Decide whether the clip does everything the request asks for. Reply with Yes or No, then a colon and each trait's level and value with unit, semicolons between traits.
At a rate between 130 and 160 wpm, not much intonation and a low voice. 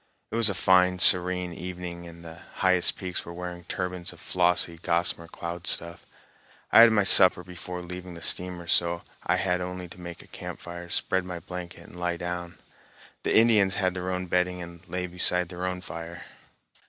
No: average, 185 wpm; narrow, 1.0 semitones; very low, 90 Hz